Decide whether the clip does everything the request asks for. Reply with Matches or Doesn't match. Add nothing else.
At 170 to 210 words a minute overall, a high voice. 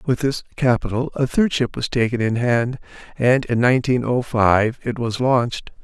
Doesn't match